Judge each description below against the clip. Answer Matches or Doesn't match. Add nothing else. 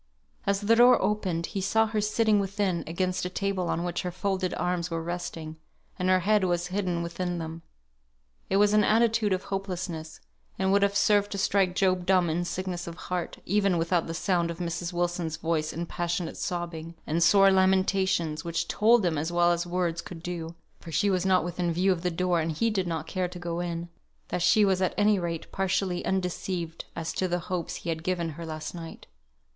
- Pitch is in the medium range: Matches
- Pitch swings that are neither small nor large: Doesn't match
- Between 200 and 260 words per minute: Matches